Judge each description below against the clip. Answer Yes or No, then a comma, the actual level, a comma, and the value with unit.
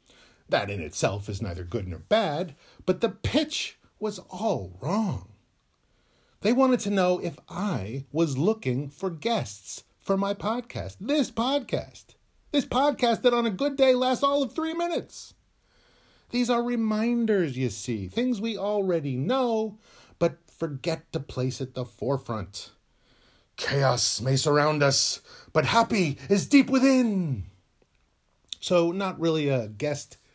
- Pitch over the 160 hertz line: Yes, medium, 185 Hz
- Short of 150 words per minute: Yes, average, 140 wpm